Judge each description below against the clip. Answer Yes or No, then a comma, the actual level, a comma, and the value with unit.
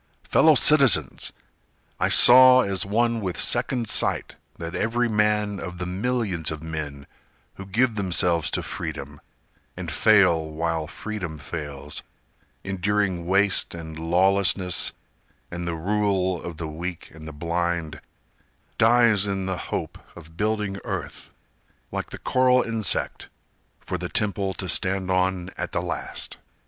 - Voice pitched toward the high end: No, very low, 95 Hz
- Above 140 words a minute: No, slow, 135 wpm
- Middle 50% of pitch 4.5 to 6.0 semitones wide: No, average, 4.1 semitones